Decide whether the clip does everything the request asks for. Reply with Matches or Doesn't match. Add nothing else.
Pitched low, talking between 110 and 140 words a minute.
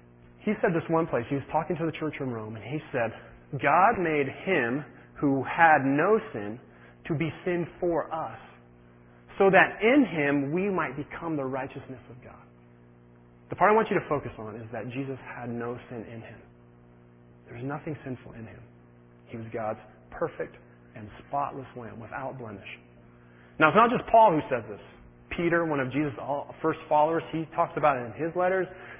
Doesn't match